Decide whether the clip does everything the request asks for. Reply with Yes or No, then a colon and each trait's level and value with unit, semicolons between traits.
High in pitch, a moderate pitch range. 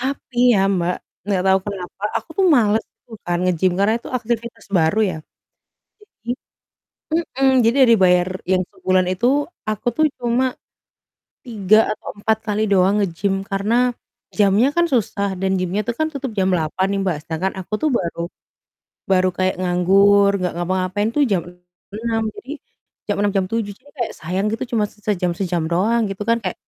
Yes: high, 200 Hz; average, 3.7 semitones